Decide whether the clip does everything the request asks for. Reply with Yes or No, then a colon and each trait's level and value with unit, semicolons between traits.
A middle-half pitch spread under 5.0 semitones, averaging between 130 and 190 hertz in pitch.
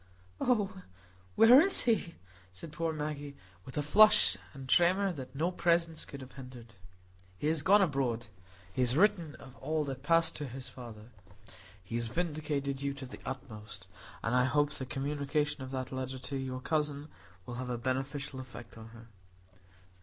Yes: average, 3.6 semitones; medium, 140 Hz